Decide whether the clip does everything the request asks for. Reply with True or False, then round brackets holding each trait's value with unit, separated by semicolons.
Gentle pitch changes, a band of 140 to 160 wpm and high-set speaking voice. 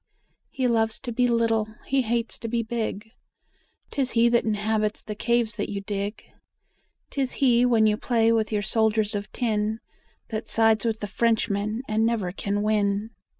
False (1.8 semitones; 170 wpm; 220 Hz)